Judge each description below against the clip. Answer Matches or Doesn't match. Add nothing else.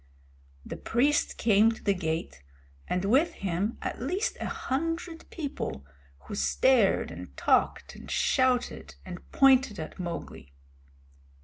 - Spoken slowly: Matches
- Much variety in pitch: Matches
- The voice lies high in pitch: Matches